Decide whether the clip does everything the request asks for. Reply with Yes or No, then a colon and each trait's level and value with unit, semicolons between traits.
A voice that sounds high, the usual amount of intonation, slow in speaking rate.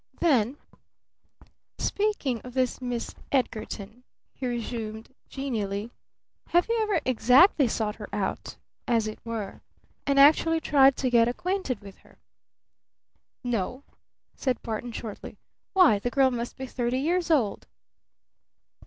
Yes: very high, 250 Hz; average, 3.9 semitones; slow, 125 wpm